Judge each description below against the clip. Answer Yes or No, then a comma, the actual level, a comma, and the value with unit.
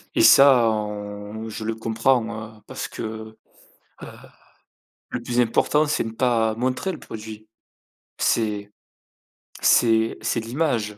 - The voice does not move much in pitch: Yes, narrow, 2.0 semitones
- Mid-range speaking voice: No, low, 110 Hz